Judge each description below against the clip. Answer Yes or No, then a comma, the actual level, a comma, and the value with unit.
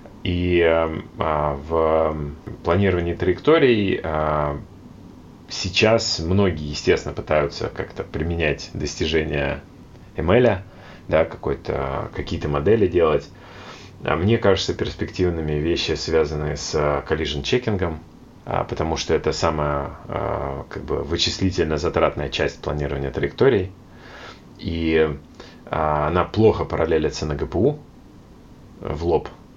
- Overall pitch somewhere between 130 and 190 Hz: No, very low, 80 Hz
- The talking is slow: Yes, slow, 90 wpm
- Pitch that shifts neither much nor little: Yes, average, 4.0 semitones